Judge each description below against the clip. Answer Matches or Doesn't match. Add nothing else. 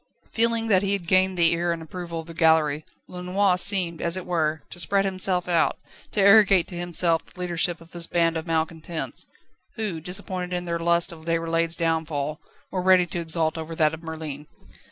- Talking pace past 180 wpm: Matches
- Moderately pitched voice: Matches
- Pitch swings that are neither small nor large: Doesn't match